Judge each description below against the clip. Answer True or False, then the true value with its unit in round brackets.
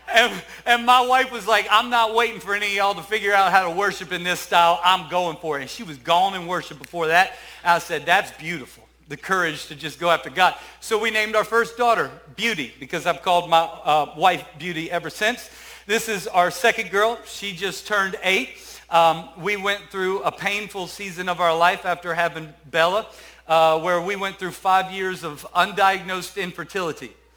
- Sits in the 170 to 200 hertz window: True (185 Hz)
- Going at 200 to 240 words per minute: True (205 wpm)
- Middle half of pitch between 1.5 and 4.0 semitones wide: True (3.5 semitones)